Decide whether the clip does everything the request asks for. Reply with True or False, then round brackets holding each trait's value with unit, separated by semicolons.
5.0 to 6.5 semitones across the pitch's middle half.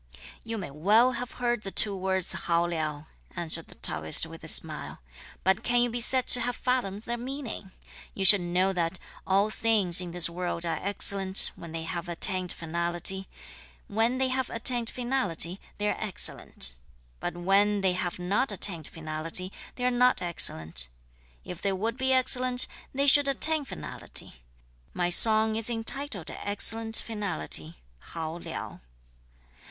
True (5.6 semitones)